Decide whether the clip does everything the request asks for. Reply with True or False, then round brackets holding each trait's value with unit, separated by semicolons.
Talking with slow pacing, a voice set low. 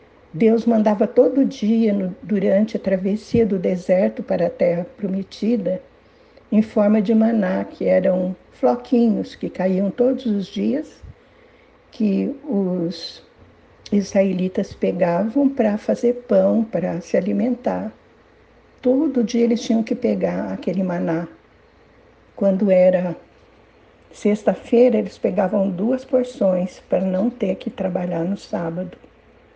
False (115 wpm; 205 Hz)